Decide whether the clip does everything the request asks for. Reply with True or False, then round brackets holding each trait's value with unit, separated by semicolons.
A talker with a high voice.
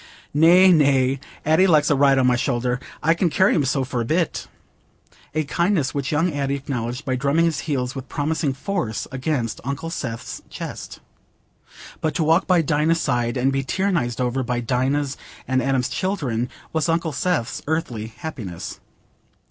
False (140 Hz)